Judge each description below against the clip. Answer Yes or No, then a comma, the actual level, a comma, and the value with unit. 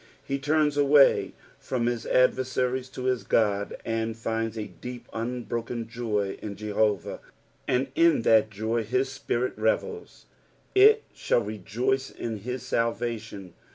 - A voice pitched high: No, low, 120 Hz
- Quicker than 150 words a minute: No, slow, 135 wpm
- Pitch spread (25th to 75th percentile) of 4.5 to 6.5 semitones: No, average, 2.8 semitones